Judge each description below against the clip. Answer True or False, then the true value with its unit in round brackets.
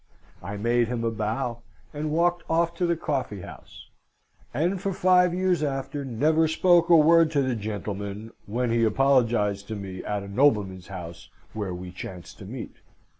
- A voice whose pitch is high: False (120 Hz)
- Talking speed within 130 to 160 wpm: False (175 wpm)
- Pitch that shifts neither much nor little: False (7.7 semitones)